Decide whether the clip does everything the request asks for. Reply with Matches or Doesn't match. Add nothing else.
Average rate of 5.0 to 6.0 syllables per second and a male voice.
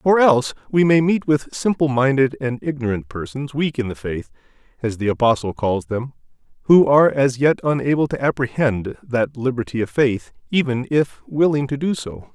Matches